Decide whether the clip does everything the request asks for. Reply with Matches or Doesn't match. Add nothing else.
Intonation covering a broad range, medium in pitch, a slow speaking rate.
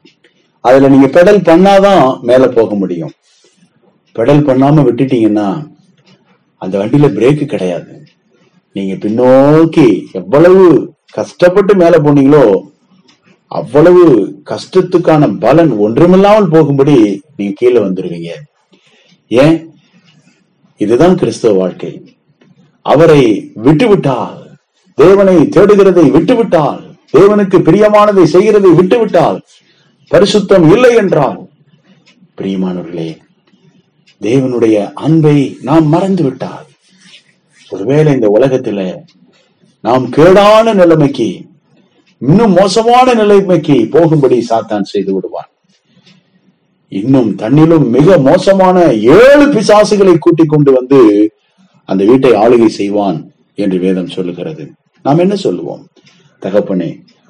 Matches